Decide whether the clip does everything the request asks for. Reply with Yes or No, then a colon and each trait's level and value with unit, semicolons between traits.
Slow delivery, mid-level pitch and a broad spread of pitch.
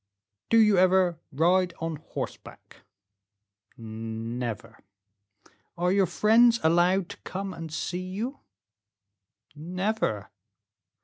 No: slow, 90 wpm; medium, 180 Hz; average, 4.0 semitones